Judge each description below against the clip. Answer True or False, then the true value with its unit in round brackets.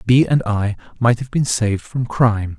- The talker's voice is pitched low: True (115 Hz)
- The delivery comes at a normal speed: False (210 wpm)